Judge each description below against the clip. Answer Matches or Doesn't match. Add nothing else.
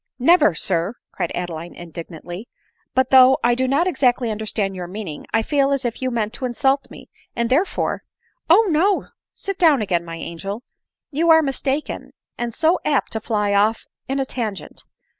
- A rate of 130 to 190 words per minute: Doesn't match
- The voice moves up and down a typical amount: Doesn't match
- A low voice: Doesn't match